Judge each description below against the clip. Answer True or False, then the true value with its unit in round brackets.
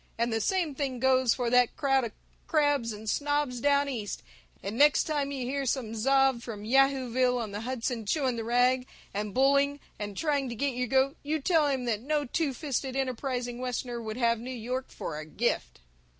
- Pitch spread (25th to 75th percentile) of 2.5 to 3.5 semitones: True (3.1 semitones)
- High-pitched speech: True (255 Hz)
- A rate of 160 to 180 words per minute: False (195 wpm)